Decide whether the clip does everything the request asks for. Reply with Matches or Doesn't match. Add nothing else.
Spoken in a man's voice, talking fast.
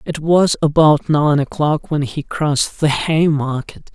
Doesn't match